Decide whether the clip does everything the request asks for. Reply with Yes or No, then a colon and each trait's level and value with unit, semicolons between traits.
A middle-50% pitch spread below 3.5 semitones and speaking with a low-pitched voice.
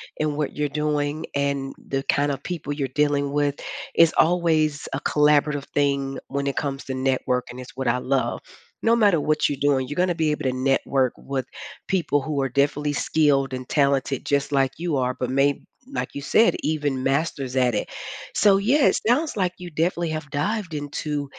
No: narrow, 2.4 semitones; medium, 145 Hz